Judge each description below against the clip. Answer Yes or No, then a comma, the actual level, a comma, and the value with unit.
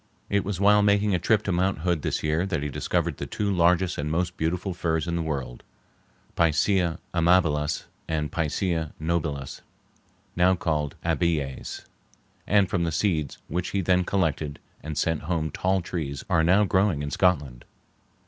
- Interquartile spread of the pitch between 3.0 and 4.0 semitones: Yes, average, 3.3 semitones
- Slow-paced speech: No, average, 160 wpm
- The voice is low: Yes, very low, 85 Hz